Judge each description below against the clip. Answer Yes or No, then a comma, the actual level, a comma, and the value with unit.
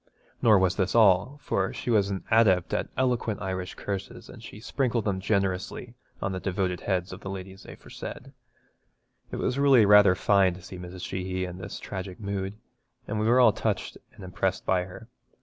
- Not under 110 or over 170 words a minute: No, average, 185 wpm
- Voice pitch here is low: Yes, very low, 95 Hz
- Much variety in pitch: No, narrow, 2.5 semitones